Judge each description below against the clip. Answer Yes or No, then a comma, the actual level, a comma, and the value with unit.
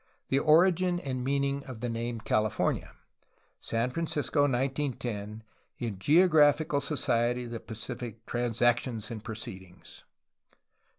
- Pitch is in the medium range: No, low, 125 Hz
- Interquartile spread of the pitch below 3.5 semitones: No, average, 3.8 semitones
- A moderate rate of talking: No, slow, 130 wpm